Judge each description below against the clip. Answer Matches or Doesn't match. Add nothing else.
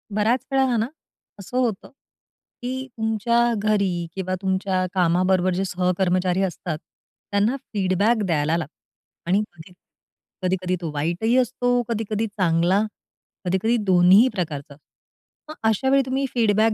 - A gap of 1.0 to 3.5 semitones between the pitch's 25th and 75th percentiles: Doesn't match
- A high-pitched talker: Matches